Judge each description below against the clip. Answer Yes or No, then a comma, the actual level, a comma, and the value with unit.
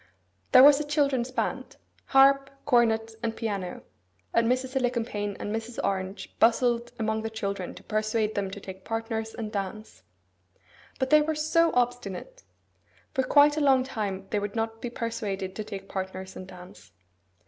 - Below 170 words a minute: Yes, average, 155 wpm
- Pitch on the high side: Yes, high, 225 Hz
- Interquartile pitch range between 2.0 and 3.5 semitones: No, average, 4.3 semitones